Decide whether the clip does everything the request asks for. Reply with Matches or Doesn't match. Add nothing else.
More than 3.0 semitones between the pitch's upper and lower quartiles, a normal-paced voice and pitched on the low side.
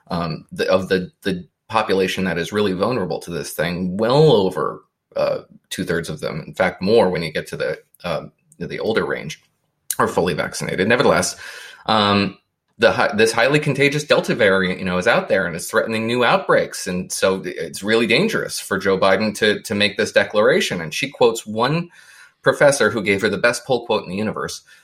Matches